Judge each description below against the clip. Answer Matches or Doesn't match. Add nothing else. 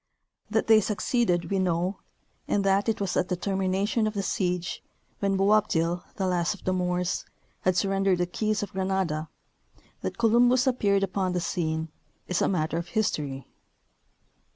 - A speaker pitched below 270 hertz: Matches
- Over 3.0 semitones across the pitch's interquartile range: Doesn't match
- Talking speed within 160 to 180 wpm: Matches